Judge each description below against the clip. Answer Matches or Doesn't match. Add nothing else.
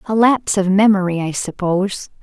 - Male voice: Doesn't match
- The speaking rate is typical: Matches